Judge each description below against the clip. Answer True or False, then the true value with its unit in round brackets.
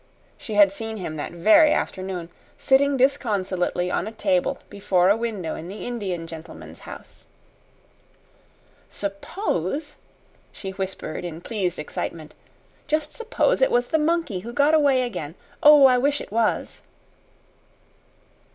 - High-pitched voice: True (210 Hz)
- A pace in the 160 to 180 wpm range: False (135 wpm)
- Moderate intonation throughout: False (7.5 semitones)